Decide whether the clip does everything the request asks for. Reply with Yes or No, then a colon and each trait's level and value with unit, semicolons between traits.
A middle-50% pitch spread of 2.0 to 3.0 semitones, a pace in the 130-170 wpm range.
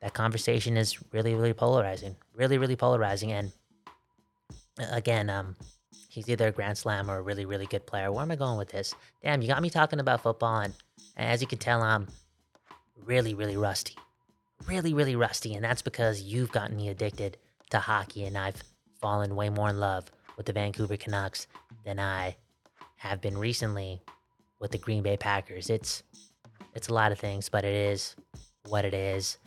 No: average, 2.7 semitones; average, 185 wpm